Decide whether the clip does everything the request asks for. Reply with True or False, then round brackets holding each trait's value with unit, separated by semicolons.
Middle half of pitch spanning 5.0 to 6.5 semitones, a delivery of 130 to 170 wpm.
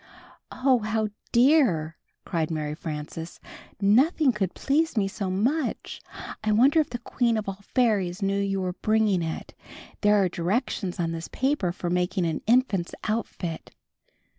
True (5.4 semitones; 150 wpm)